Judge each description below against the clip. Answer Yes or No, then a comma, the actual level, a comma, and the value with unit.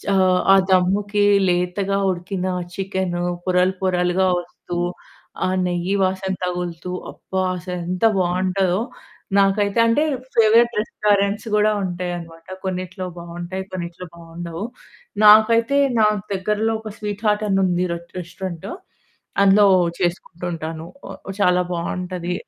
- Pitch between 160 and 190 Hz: Yes, medium, 185 Hz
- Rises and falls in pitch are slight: Yes, narrow, 2.3 semitones